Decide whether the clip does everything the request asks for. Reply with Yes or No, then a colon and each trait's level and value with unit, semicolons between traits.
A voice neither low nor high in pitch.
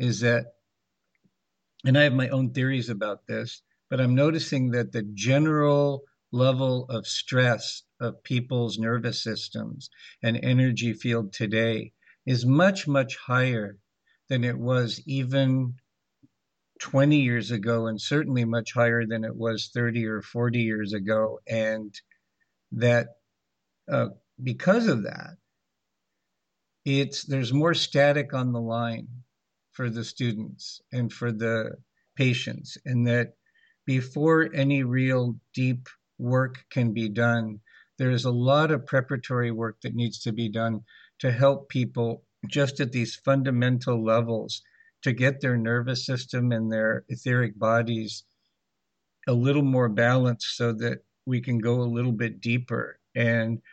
No: low, 120 Hz